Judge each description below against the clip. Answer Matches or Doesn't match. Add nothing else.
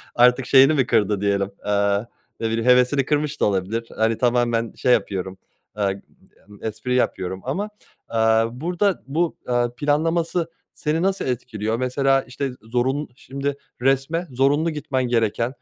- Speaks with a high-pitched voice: Doesn't match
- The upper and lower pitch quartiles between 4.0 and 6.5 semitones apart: Matches